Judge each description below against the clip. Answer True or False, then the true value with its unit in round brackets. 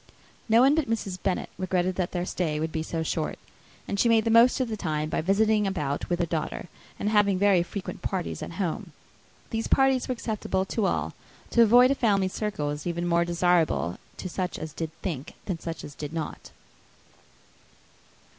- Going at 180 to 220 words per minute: True (195 wpm)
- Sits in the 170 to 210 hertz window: True (185 Hz)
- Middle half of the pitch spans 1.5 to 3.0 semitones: False (4.6 semitones)